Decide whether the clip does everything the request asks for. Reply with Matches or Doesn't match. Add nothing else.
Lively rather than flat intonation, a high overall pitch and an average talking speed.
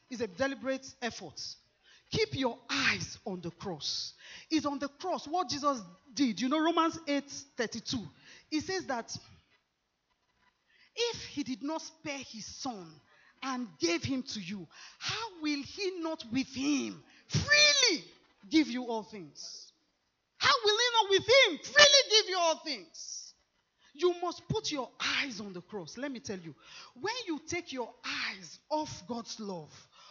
Matches